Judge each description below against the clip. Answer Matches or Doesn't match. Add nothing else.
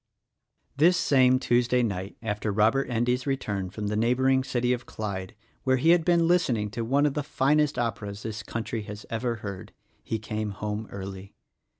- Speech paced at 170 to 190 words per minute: Matches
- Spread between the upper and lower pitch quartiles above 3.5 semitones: Matches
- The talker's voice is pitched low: Matches